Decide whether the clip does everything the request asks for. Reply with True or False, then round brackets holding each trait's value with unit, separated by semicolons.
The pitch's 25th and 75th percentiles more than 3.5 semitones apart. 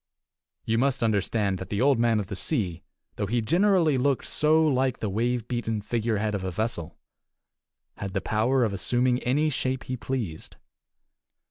True (4.2 semitones)